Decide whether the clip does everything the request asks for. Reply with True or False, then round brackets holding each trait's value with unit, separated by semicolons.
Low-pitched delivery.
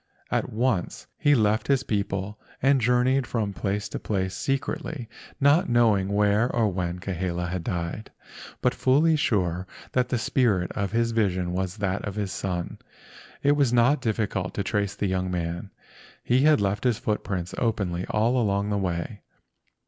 True (105 Hz)